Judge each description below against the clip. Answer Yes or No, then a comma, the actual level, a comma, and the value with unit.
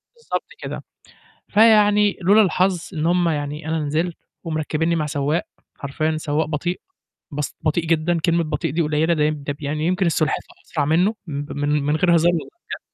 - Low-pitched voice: No, medium, 160 Hz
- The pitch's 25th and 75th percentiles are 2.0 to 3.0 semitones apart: Yes, narrow, 2.5 semitones